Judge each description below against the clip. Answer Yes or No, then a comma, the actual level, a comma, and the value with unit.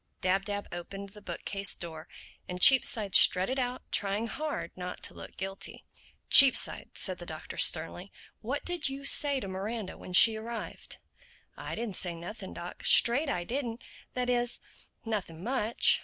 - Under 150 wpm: No, average, 155 wpm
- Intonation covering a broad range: No, average, 4.9 semitones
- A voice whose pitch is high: Yes, high, 210 Hz